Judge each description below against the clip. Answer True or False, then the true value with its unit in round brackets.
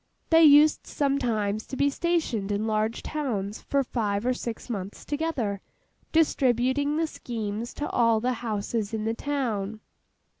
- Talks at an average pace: True (145 wpm)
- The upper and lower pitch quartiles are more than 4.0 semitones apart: True (4.9 semitones)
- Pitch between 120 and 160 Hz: False (235 Hz)